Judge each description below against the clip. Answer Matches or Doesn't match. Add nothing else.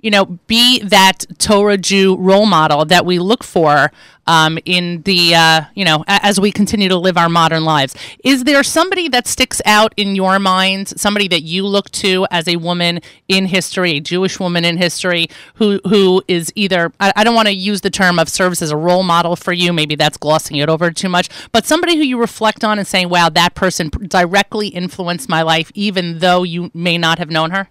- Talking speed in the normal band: Doesn't match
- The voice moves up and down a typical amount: Matches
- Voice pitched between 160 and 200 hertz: Matches